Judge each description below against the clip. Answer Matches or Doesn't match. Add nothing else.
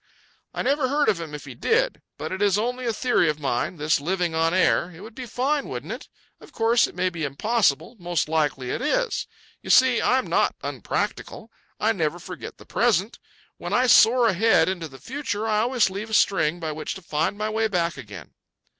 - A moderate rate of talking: Doesn't match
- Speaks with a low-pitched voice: Doesn't match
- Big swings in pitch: Matches